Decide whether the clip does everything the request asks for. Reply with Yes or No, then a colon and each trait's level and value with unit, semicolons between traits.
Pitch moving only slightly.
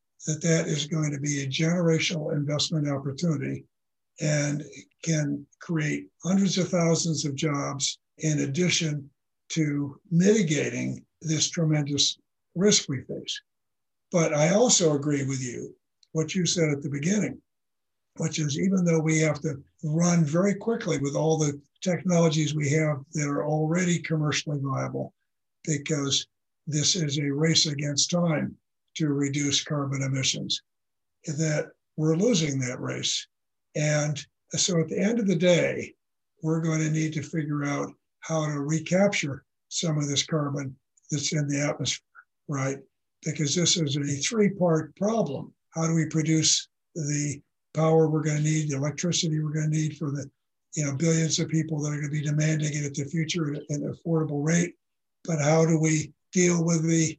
Yes: narrow, 2.3 semitones